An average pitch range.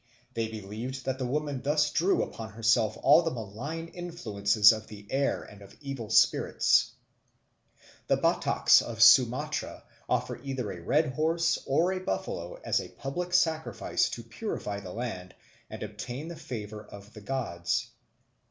No: wide, 6.1 semitones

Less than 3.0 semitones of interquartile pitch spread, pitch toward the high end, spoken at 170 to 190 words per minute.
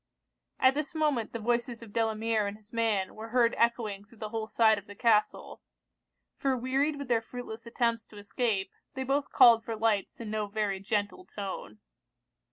Yes: narrow, 2.4 semitones; high, 225 Hz; average, 180 wpm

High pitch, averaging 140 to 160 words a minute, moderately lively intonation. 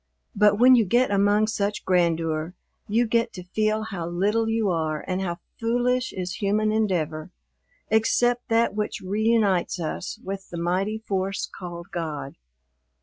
Yes: high, 200 Hz; average, 145 wpm; average, 3.9 semitones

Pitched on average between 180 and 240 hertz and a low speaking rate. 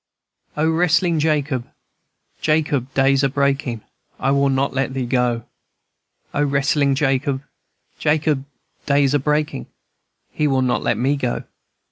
No: medium, 140 Hz; slow, 130 wpm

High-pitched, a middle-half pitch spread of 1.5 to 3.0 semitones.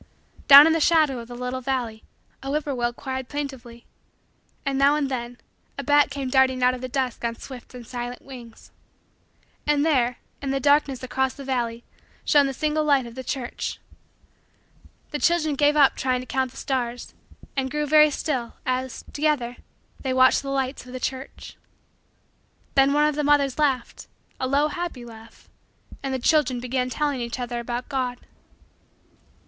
Yes: very high, 265 Hz; narrow, 2.6 semitones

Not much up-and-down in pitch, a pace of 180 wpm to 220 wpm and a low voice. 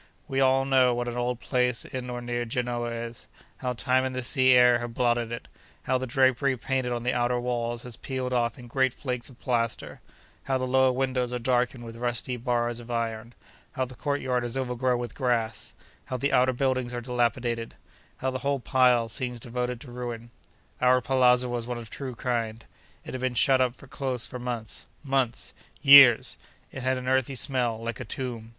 Yes: narrow, 1.4 semitones; average, 185 wpm; low, 125 Hz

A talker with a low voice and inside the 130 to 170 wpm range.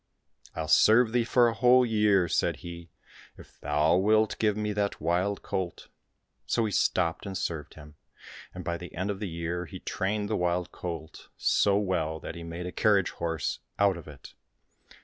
No: very low, 90 Hz; average, 190 wpm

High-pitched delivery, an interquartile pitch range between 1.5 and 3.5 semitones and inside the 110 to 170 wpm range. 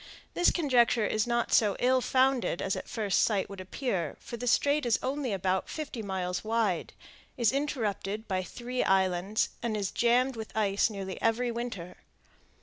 No: high, 225 Hz; average, 4.1 semitones; average, 165 wpm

